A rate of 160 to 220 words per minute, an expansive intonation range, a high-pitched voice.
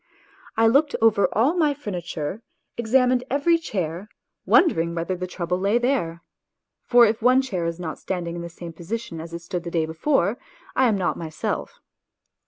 Yes: average, 175 wpm; wide, 6.4 semitones; high, 195 Hz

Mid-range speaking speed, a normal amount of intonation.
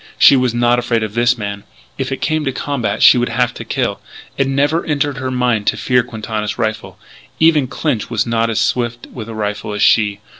No: fast, 215 wpm; average, 3.4 semitones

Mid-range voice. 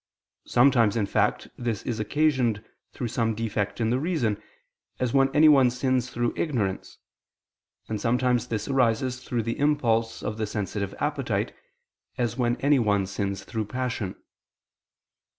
No: low, 120 Hz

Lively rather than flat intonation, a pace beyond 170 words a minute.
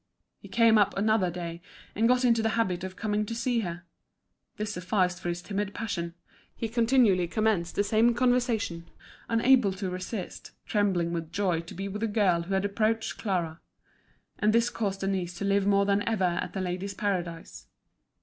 No: average, 3.7 semitones; average, 180 wpm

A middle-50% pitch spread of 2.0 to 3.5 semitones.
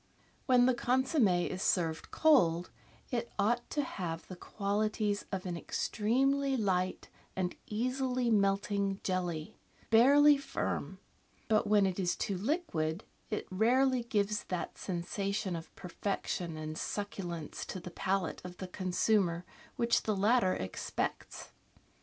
No: average, 4.8 semitones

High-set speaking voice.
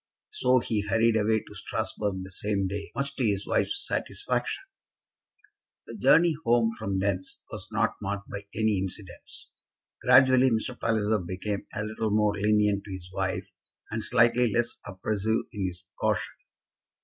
No: low, 105 Hz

